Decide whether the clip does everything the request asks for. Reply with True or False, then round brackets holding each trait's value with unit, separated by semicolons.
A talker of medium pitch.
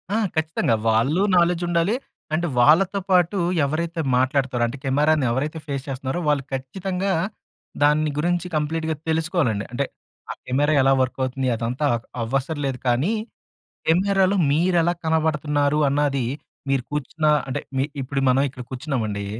True (150 Hz)